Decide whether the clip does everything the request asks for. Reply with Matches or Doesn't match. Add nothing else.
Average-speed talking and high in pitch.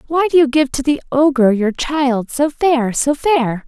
Doesn't match